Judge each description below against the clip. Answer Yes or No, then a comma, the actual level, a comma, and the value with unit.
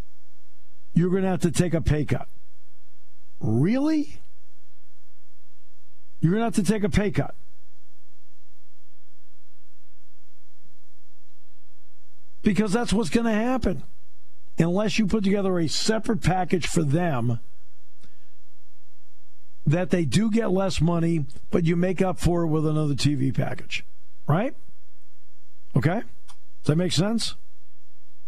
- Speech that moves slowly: Yes, slow, 120 wpm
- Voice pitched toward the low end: No, medium, 160 Hz